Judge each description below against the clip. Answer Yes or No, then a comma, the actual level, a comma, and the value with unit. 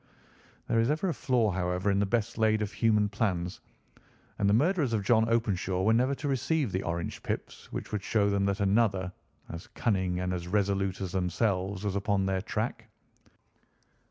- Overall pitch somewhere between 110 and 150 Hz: No, low, 100 Hz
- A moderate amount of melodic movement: Yes, average, 3.3 semitones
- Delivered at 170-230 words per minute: Yes, average, 185 wpm